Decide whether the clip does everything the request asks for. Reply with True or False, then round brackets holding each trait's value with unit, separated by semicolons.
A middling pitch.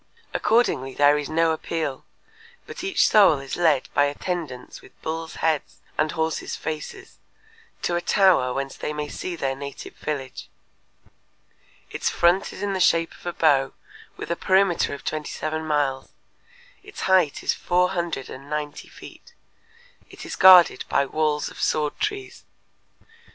True (155 Hz)